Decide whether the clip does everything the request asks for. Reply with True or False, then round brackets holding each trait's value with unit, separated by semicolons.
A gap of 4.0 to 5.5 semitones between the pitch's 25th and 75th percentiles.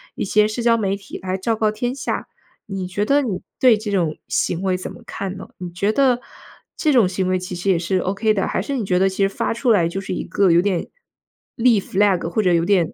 False (3.0 semitones)